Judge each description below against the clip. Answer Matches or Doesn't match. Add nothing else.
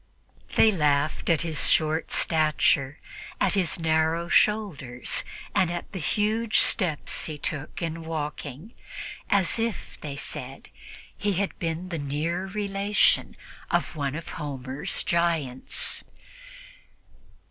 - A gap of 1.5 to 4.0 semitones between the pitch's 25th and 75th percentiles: Doesn't match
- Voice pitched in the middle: Matches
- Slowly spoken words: Matches